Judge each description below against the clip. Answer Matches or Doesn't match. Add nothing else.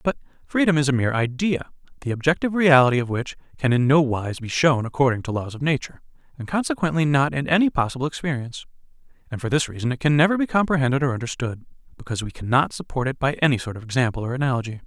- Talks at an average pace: Doesn't match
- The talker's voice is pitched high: Doesn't match